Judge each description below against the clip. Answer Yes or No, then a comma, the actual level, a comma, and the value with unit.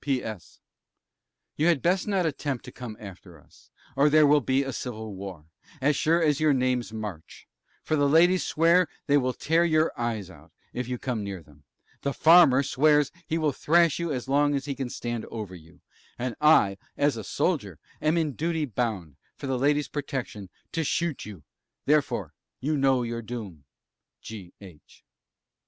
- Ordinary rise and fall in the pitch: No, wide, 5.8 semitones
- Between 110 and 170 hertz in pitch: Yes, low, 135 Hz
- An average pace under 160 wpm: No, average, 180 wpm